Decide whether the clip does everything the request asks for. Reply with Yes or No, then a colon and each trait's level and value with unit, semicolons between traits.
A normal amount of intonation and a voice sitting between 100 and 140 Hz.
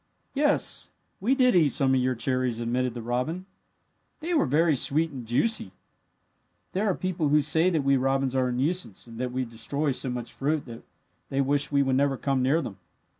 Yes: average, 4.1 semitones; low, 135 Hz